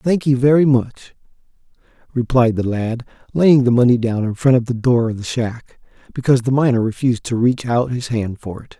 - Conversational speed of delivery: No, fast, 210 wpm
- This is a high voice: No, low, 125 Hz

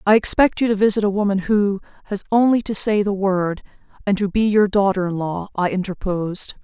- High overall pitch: Yes, high, 200 Hz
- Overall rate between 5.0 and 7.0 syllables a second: Yes, 5.5 syllables/s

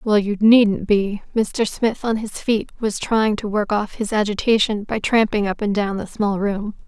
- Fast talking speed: Yes, fast, 210 wpm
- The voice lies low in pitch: No, high, 210 Hz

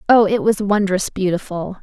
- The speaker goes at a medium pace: Yes, average, 165 wpm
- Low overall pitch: No, high, 195 Hz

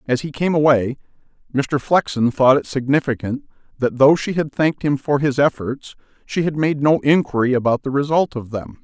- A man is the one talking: Yes, male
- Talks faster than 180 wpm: Yes, average, 190 wpm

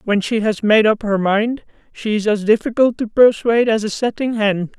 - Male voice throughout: No, female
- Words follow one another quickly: Yes, fast, 215 wpm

